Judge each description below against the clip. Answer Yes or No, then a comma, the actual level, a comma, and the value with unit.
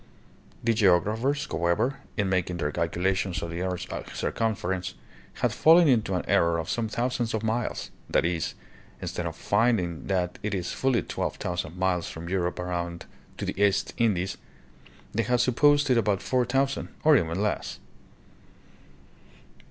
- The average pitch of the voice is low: Yes, very low, 95 Hz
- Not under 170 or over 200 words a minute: No, average, 160 wpm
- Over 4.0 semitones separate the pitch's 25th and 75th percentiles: Yes, average, 5.0 semitones